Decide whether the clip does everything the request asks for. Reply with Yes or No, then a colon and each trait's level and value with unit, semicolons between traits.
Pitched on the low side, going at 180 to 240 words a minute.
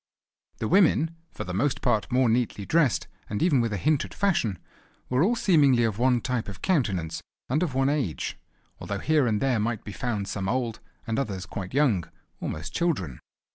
Yes: low, 120 Hz; average, 190 wpm